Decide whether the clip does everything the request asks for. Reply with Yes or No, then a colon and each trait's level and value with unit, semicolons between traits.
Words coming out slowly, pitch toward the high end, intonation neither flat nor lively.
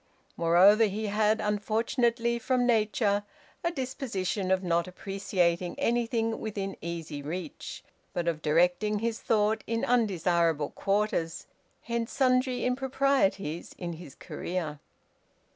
Yes: slow, 110 wpm; high, 205 Hz; average, 5.0 semitones